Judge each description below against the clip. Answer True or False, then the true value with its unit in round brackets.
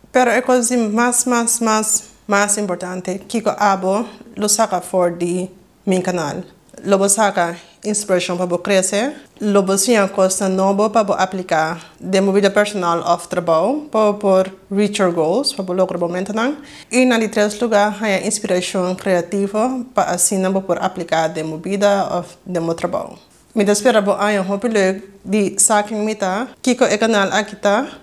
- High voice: True (200 Hz)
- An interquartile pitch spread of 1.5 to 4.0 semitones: True (2.8 semitones)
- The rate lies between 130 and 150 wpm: True (135 wpm)